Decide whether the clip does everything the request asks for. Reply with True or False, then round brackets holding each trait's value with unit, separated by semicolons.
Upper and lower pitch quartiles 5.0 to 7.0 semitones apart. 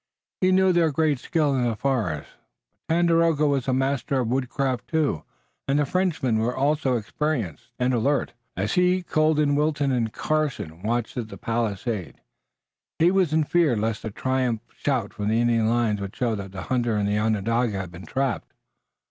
True (5.3 semitones)